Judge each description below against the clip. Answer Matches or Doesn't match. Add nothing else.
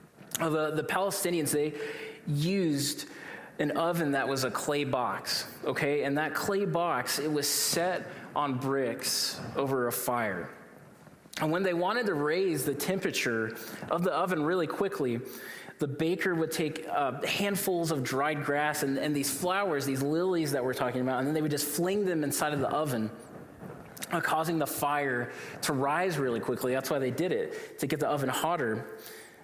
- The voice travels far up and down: Doesn't match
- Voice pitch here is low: Doesn't match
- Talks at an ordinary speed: Matches